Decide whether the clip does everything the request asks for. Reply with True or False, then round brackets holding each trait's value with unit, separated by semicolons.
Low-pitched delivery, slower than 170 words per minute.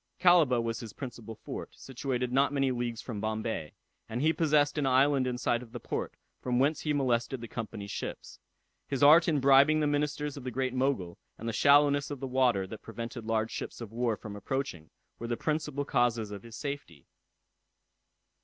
False (125 Hz; 190 wpm)